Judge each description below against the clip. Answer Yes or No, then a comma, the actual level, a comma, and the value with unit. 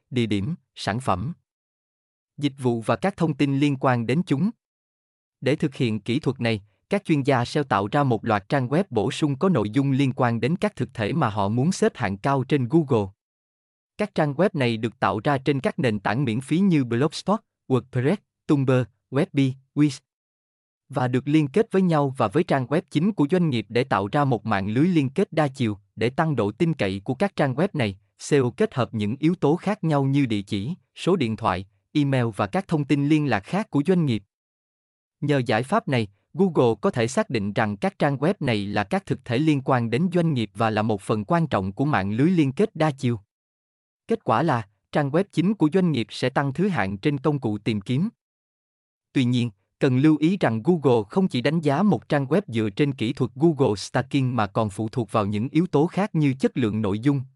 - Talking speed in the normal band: Yes, average, 225 wpm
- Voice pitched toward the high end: No, low, 135 Hz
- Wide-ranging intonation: Yes, wide, 5.9 semitones